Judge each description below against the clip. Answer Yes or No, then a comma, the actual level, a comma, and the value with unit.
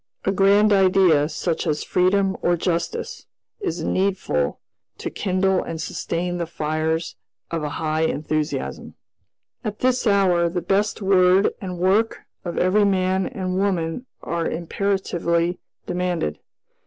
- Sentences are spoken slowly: Yes, slow, 130 wpm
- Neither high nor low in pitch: Yes, medium, 180 Hz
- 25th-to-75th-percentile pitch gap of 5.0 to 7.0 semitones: No, average, 2.8 semitones